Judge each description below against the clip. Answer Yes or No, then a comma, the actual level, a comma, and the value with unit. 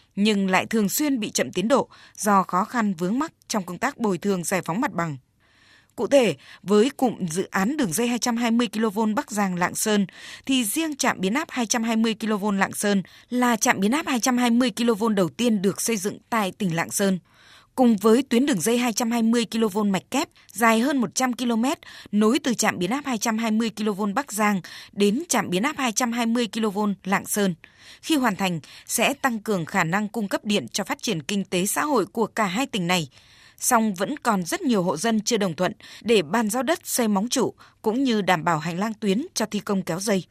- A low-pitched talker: No, high, 220 Hz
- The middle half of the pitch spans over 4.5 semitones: No, average, 3.8 semitones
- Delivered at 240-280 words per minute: No, average, 210 wpm